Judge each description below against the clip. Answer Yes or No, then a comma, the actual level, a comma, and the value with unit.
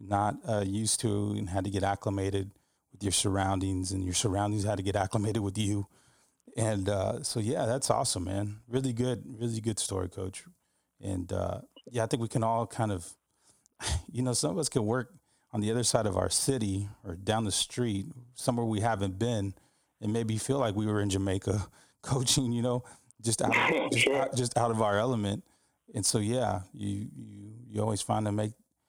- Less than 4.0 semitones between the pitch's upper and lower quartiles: Yes, average, 3.2 semitones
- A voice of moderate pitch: No, low, 105 Hz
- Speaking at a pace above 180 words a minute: Yes, average, 200 wpm